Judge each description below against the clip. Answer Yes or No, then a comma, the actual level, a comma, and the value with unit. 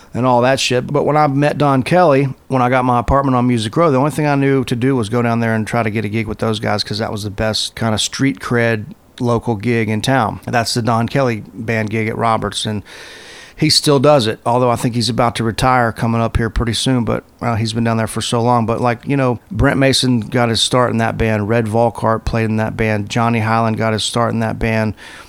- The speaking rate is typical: No, fast, 265 wpm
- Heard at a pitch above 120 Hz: No, low, 115 Hz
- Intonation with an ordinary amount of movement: No, narrow, 2.2 semitones